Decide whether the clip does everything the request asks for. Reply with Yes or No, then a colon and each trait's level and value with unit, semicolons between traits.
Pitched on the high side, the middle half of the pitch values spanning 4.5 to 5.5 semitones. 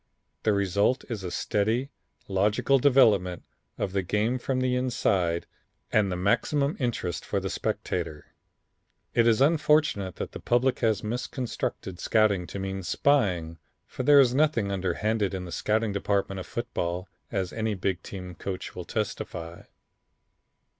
No: low, 105 Hz; average, 4.9 semitones